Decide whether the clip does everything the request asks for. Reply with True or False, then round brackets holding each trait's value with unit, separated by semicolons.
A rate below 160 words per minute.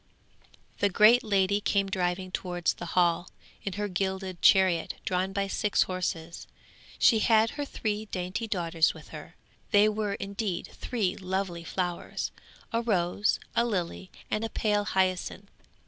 True (145 wpm)